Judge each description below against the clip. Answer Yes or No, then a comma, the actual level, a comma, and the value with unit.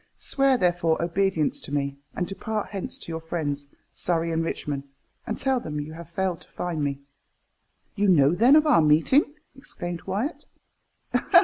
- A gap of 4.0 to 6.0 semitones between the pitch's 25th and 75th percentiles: Yes, average, 4.5 semitones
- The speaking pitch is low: No, medium, 170 Hz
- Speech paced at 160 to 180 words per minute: Yes, average, 165 wpm